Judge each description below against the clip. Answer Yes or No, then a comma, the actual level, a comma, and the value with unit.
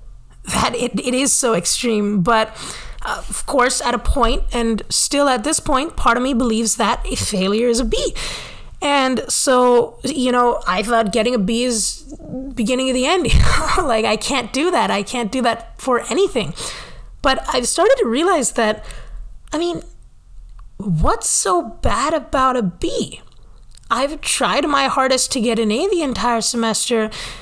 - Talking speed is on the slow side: No, average, 175 wpm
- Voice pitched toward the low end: No, high, 245 Hz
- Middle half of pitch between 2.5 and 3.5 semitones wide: Yes, average, 3.1 semitones